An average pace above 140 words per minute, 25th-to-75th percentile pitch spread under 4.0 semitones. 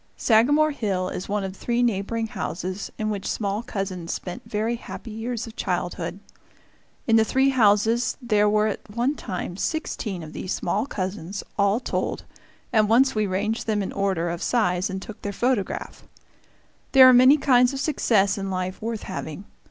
Yes: average, 175 wpm; average, 3.6 semitones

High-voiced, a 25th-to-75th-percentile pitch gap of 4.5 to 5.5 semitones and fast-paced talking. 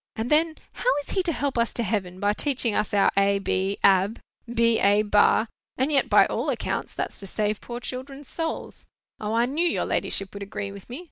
Yes: high, 225 Hz; average, 5.0 semitones; fast, 210 wpm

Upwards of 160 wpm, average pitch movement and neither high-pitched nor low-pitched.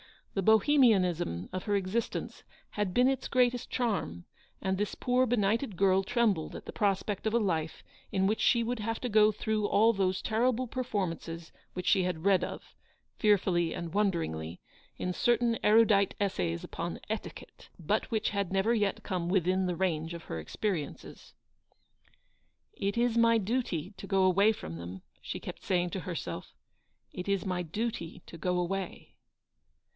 No: average, 170 wpm; average, 3.8 semitones; high, 195 Hz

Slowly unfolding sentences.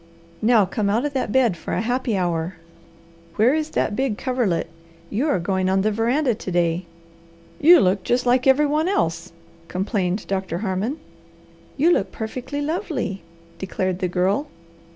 No: average, 160 wpm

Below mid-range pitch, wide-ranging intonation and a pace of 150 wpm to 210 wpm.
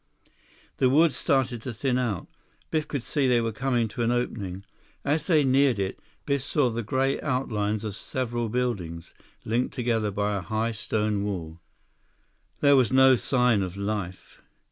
No: low, 120 Hz; average, 4.2 semitones; average, 165 wpm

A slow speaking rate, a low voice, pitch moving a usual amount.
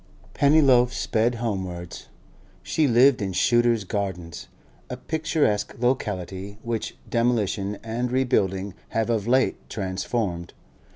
Yes: slow, 105 wpm; low, 115 Hz; average, 4.2 semitones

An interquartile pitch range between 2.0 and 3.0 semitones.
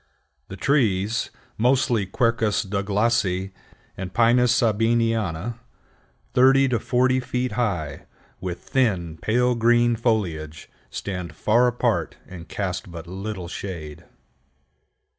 No: average, 4.5 semitones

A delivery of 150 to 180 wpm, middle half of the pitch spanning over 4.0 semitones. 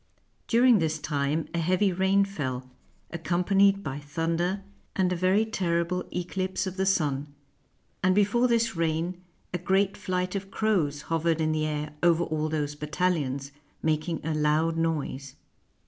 No: average, 160 wpm; average, 3.7 semitones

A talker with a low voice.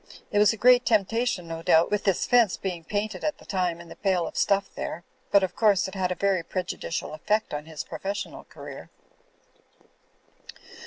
No: high, 195 Hz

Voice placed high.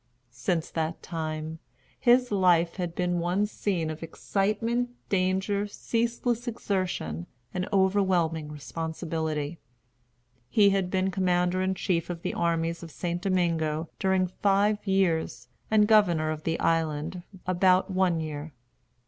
No: medium, 180 Hz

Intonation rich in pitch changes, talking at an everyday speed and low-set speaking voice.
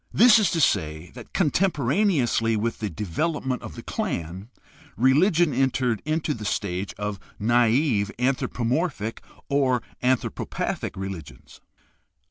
No: wide, 6.2 semitones; slow, 120 wpm; low, 125 Hz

